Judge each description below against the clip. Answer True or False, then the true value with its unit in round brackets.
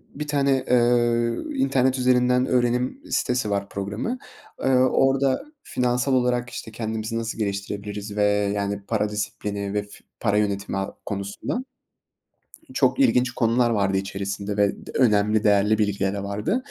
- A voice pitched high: False (110 Hz)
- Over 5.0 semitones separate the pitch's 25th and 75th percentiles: False (3.7 semitones)